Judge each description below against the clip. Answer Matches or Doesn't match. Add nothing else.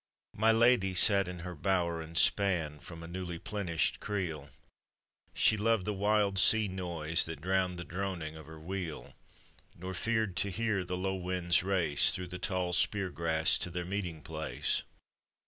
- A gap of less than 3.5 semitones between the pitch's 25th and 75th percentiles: Matches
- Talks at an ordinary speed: Matches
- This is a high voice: Doesn't match